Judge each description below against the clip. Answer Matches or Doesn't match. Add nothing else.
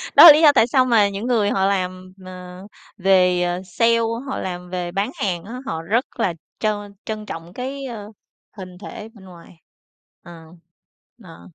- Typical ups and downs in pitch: Matches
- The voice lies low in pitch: Doesn't match